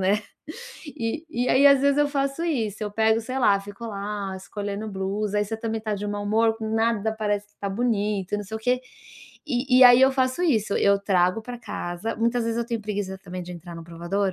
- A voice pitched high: Yes, high, 215 Hz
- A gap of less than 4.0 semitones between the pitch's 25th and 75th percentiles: Yes, average, 3.3 semitones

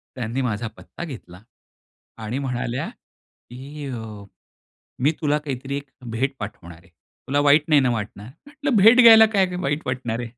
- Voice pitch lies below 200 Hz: Yes, low, 135 Hz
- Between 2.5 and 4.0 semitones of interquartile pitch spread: No, average, 4.4 semitones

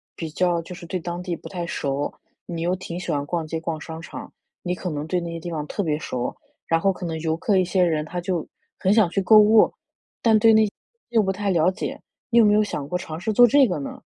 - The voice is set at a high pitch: No, medium, 175 Hz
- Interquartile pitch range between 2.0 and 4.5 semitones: Yes, average, 3.5 semitones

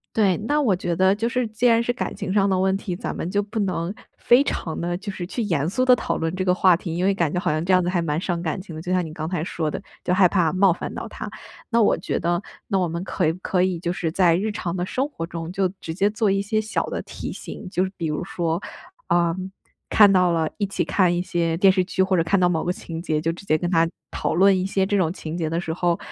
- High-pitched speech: No, medium, 180 Hz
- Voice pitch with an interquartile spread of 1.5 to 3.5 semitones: Yes, average, 2.8 semitones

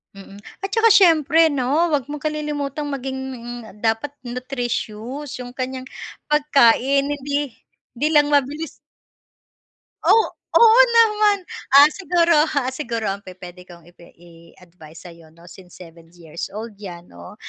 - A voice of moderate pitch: No, very high, 260 Hz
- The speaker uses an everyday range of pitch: No, wide, 8.2 semitones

